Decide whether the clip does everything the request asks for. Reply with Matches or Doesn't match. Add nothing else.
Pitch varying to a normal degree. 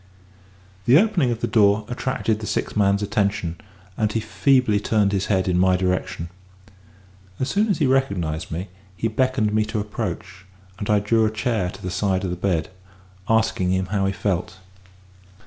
Matches